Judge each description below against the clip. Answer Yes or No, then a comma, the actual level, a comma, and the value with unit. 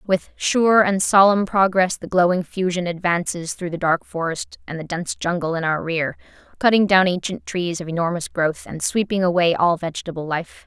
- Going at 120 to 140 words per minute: No, average, 185 wpm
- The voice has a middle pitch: Yes, medium, 175 Hz